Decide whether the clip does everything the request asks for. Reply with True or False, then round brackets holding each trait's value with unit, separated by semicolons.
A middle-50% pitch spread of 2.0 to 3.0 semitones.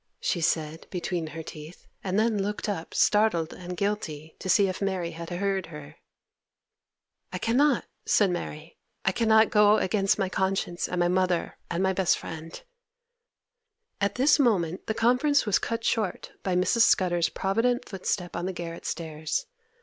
False (3.7 semitones)